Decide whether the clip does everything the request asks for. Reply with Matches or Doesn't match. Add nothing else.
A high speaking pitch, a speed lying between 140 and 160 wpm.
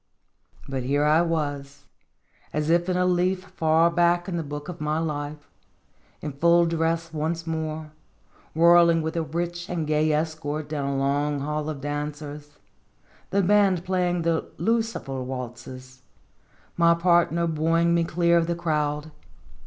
Doesn't match